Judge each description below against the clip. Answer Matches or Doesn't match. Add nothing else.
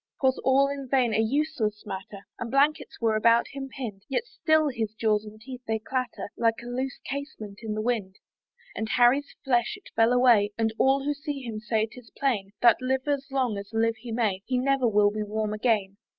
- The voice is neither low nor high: Doesn't match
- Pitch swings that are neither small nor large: Matches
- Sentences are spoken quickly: Matches